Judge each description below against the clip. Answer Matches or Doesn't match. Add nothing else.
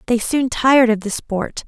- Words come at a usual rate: Doesn't match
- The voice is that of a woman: Matches